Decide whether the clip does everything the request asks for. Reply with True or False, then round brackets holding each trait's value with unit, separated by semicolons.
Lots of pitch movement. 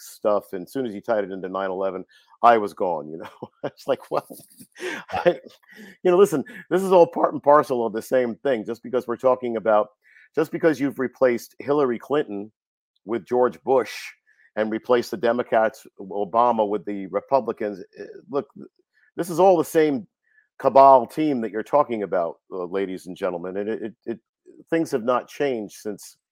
True (7.1 semitones)